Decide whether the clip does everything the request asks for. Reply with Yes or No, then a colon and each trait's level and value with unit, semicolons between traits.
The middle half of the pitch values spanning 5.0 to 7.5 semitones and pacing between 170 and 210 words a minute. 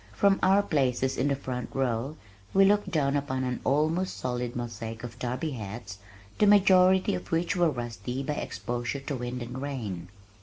Yes: average, 5.3 semitones; average, 175 wpm